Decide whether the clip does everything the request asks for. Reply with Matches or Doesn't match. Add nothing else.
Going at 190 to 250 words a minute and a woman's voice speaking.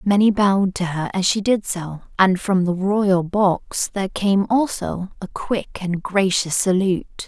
Doesn't match